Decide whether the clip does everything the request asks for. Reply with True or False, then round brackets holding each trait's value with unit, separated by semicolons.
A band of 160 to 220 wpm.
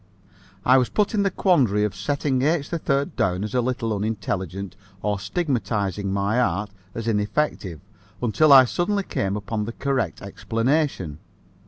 False (150 wpm)